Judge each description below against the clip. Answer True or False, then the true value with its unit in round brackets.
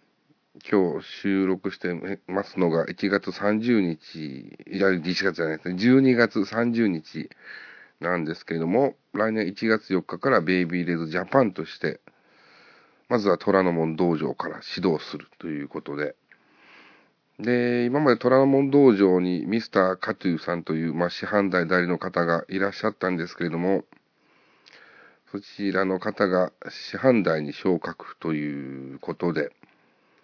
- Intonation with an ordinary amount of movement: True (3.8 semitones)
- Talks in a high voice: False (95 Hz)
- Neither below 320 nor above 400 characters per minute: False (265 characters per minute)